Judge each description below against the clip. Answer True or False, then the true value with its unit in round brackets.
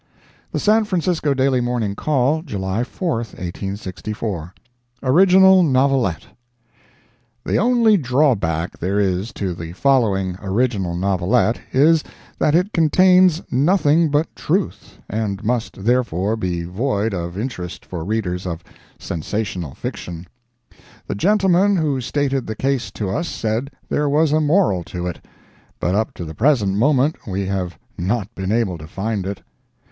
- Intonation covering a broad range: True (7.8 semitones)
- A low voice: True (115 Hz)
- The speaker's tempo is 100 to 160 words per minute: True (140 wpm)